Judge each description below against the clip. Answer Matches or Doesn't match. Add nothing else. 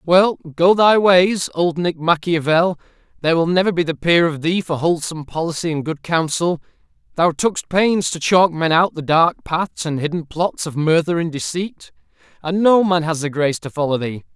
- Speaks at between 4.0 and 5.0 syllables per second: Matches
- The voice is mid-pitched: Matches